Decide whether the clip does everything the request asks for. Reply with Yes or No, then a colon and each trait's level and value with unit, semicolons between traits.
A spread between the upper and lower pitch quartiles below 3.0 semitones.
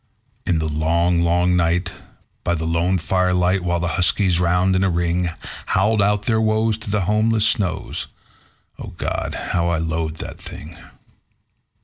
Yes: narrow, 2.6 semitones